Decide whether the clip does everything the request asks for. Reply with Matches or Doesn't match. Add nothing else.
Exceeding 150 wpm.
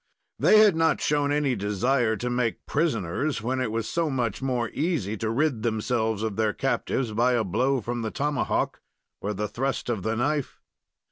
Matches